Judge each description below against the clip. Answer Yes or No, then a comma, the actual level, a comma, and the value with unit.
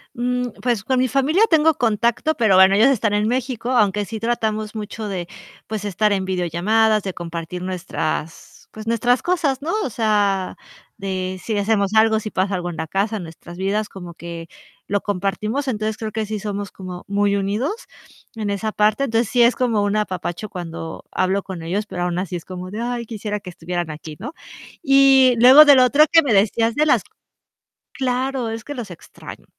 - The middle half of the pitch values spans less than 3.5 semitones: No, average, 4.2 semitones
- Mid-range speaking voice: No, high, 215 Hz